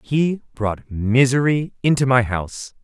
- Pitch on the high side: No, low, 125 Hz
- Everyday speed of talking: No, slow, 125 wpm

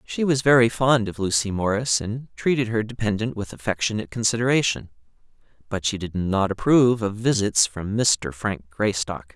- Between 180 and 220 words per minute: No, average, 155 wpm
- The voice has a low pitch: Yes, low, 110 Hz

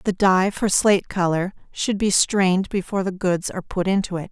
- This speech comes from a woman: Yes, female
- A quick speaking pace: Yes, fast, 210 wpm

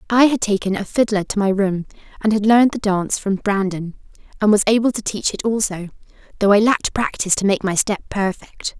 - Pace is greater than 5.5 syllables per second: Yes, 5.8 syllables/s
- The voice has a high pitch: Yes, high, 205 Hz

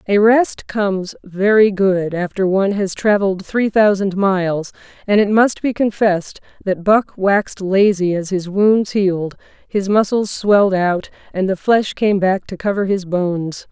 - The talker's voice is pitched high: Yes, high, 195 Hz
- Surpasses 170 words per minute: No, average, 165 wpm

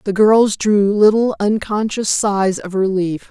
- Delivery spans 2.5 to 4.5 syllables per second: Yes, 3.9 syllables/s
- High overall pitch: Yes, high, 205 Hz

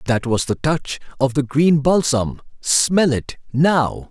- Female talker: No, male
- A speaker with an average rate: Yes, average, 145 wpm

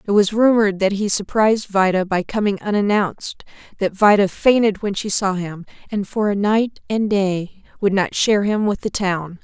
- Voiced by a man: No, female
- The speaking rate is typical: Yes, average, 190 wpm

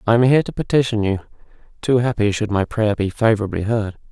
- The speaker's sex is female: No, male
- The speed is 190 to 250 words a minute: Yes, fast, 205 wpm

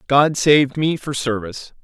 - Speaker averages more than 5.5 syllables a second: No, 5.0 syllables/s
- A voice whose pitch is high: No, medium, 140 Hz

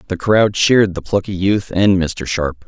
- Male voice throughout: Yes, male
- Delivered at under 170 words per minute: No, average, 200 wpm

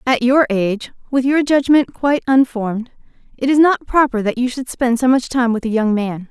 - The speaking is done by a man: No, female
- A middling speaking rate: No, fast, 220 wpm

